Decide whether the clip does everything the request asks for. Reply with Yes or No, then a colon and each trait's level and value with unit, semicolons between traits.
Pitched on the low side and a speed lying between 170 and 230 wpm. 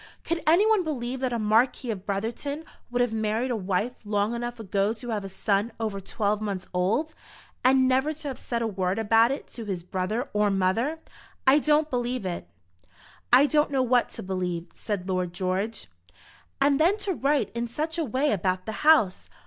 No: high, 230 Hz; average, 190 wpm